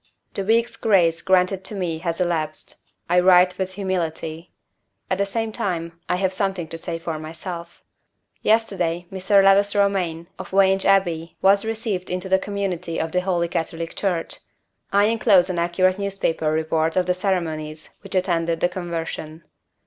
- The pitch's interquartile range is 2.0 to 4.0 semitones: Yes, average, 2.8 semitones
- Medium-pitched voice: Yes, medium, 180 Hz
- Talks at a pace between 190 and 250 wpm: No, average, 160 wpm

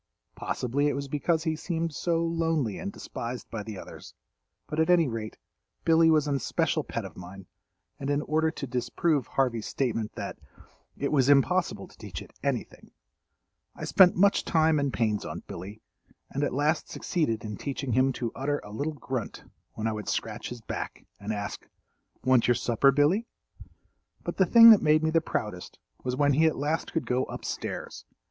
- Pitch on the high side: No, medium, 140 Hz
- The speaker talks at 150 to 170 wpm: No, average, 185 wpm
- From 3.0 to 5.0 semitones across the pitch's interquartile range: No, wide, 5.4 semitones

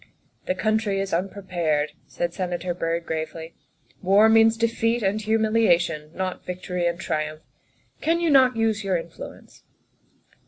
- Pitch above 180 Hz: Yes, high, 190 Hz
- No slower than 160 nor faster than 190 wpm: No, average, 150 wpm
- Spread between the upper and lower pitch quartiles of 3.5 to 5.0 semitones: Yes, average, 4.4 semitones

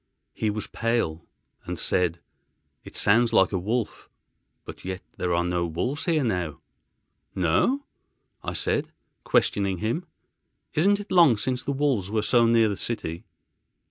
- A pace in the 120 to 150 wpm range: Yes, average, 140 wpm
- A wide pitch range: Yes, wide, 5.7 semitones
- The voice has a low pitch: Yes, low, 110 Hz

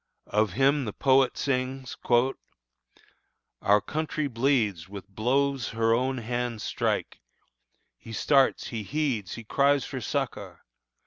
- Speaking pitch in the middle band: No, low, 125 Hz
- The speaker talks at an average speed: No, slow, 120 wpm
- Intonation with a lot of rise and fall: No, average, 3.9 semitones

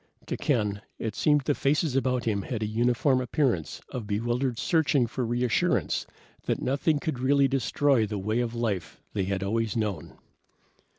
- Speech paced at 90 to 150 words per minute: No, average, 165 wpm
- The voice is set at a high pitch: No, low, 120 Hz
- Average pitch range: Yes, average, 3.9 semitones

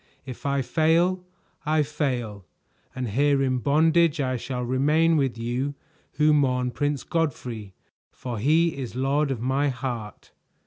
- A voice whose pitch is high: No, low, 135 Hz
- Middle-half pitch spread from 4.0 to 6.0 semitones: No, average, 3.2 semitones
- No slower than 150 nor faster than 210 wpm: No, average, 140 wpm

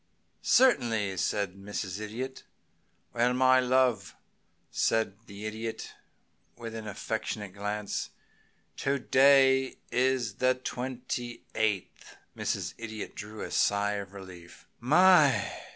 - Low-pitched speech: Yes, low, 115 Hz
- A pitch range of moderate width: Yes, average, 4.0 semitones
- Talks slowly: Yes, slow, 115 wpm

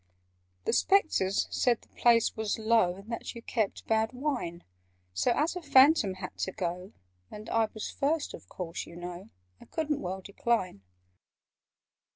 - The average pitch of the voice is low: No, high, 220 Hz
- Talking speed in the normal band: Yes, average, 160 wpm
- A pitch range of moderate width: No, wide, 5.7 semitones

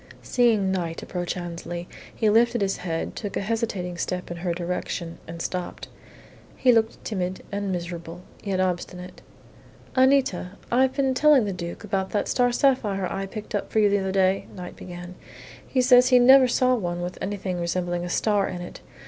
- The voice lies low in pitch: No, high, 190 Hz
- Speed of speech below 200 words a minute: Yes, average, 180 wpm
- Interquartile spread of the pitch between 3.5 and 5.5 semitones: Yes, average, 4.6 semitones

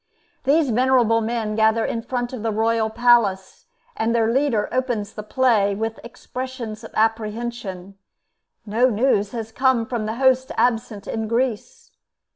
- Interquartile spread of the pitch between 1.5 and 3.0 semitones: Yes, narrow, 2.6 semitones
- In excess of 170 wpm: No, average, 145 wpm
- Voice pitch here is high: Yes, high, 230 Hz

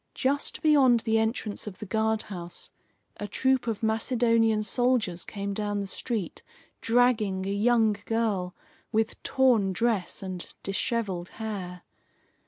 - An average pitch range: Yes, average, 3.0 semitones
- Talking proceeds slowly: Yes, slow, 125 wpm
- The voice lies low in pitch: No, high, 220 Hz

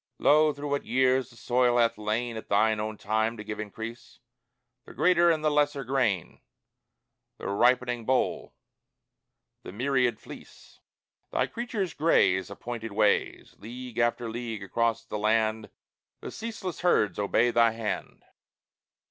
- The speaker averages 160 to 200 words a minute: No, average, 140 wpm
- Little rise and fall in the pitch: No, average, 3.3 semitones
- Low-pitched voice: Yes, low, 120 Hz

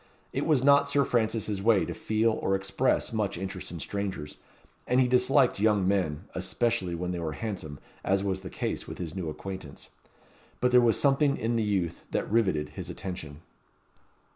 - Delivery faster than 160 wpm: Yes, average, 180 wpm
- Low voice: Yes, low, 100 Hz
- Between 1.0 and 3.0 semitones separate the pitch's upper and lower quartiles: No, average, 4.4 semitones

